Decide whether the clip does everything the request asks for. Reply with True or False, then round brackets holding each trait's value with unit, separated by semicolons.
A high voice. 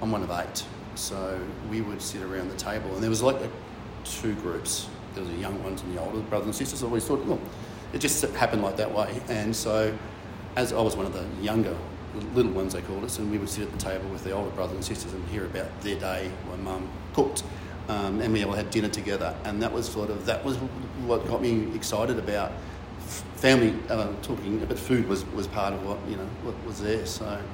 False (105 Hz)